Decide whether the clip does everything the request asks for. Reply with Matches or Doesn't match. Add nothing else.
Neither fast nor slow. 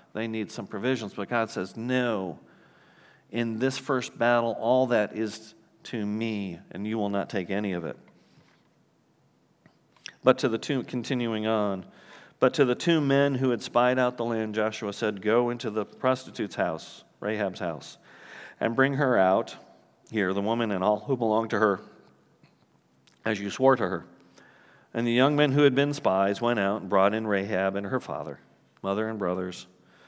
Matches